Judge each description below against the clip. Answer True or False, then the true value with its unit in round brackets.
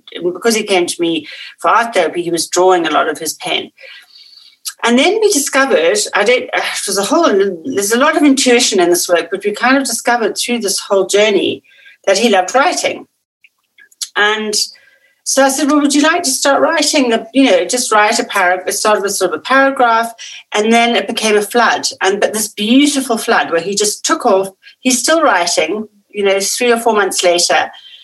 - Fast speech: True (210 wpm)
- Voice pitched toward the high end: True (230 Hz)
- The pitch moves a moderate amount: False (5.8 semitones)